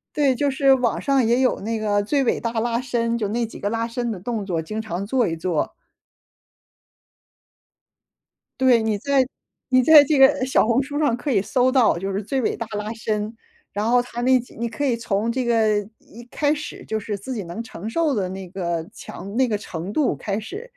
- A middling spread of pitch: Yes, average, 3.8 semitones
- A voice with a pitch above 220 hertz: Yes, high, 230 Hz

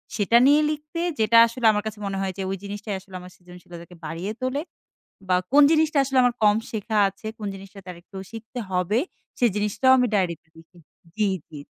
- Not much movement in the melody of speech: No, average, 4.3 semitones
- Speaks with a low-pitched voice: No, high, 205 Hz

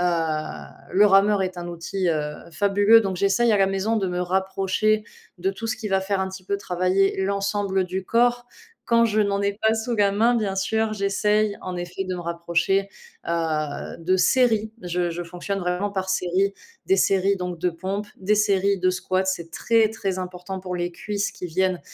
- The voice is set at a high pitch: Yes, high, 195 Hz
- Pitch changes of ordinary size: No, narrow, 2.3 semitones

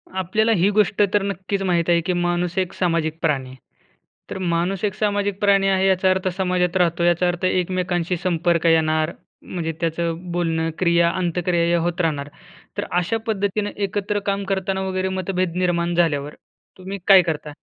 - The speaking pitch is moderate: Yes, medium, 180 Hz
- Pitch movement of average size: No, narrow, 2.1 semitones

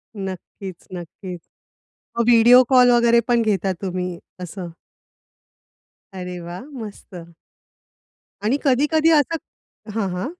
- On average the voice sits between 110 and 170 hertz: No, high, 205 Hz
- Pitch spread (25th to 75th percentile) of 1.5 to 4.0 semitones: No, average, 5.0 semitones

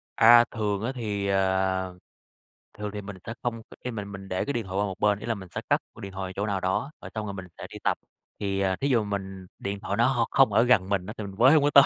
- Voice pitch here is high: No, low, 100 Hz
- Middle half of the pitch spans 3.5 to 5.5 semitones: No, average, 3.1 semitones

